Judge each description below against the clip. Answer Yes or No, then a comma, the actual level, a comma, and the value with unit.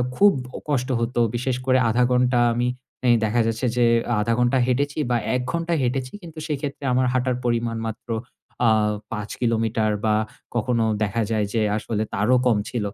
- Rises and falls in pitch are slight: Yes, narrow, 2.2 semitones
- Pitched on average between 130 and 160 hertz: No, low, 120 Hz